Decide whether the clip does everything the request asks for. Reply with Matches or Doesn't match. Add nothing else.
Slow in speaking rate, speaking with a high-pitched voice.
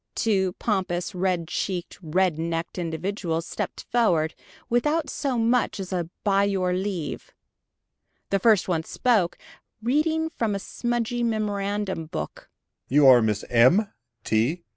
Matches